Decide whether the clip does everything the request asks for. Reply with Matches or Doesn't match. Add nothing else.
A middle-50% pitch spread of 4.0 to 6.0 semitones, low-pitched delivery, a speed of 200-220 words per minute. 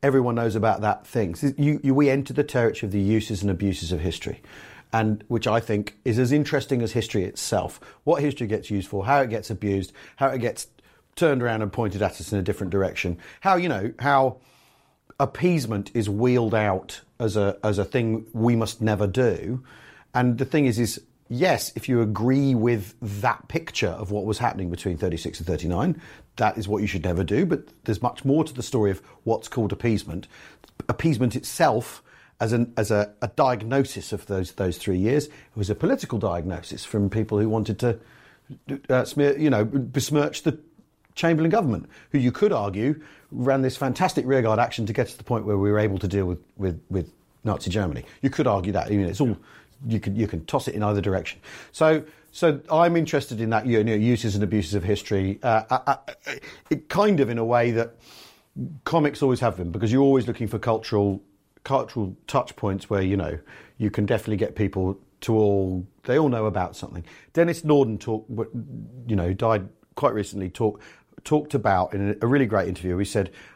Matches